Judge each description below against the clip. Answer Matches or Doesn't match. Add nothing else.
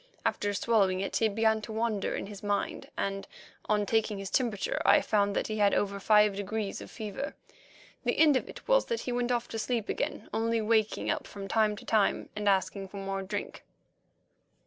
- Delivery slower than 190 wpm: Doesn't match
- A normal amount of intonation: Doesn't match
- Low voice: Doesn't match